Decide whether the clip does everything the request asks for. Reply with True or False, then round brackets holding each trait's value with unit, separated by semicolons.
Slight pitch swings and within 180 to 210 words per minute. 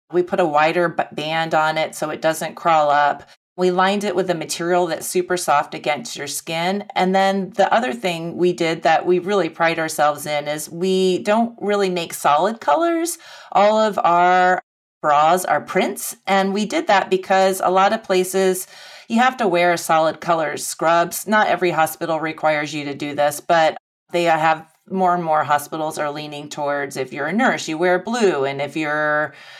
False (3.5 semitones; 190 wpm)